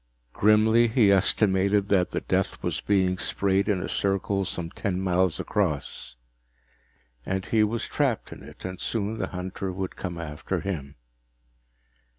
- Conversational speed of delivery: Yes, average, 150 wpm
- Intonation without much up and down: Yes, narrow, 2.3 semitones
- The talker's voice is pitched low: Yes, very low, 95 Hz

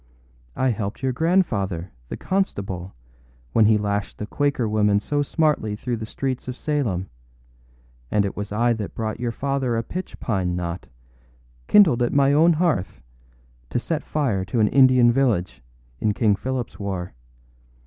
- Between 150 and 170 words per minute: Yes, average, 160 wpm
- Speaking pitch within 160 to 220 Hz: No, low, 115 Hz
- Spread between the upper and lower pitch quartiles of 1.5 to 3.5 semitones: No, average, 5.2 semitones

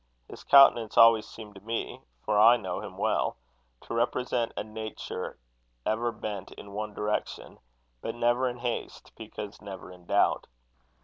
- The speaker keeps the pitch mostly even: Yes, narrow, 2.2 semitones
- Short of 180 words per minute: Yes, average, 150 wpm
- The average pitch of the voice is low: Yes, low, 110 Hz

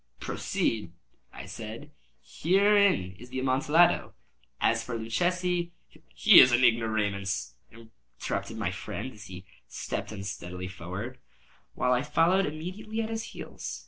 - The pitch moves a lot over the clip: Yes, wide, 8.6 semitones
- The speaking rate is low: Yes, slow, 125 wpm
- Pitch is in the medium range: No, low, 120 Hz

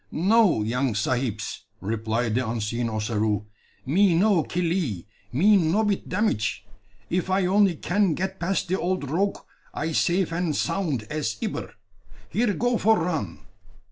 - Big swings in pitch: Yes, wide, 8.8 semitones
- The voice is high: No, medium, 165 Hz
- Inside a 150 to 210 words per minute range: No, average, 140 wpm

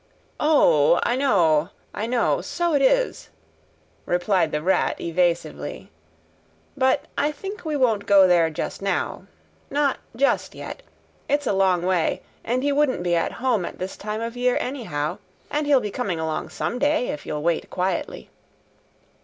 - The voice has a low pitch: No, high, 210 Hz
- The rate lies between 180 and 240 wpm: No, average, 160 wpm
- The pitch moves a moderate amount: No, wide, 8.0 semitones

